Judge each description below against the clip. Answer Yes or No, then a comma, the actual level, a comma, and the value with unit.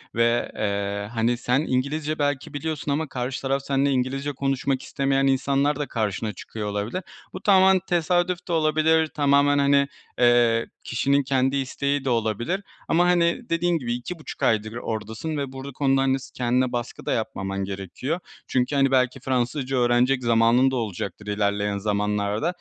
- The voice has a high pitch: No, low, 130 Hz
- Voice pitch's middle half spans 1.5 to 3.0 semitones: No, average, 3.7 semitones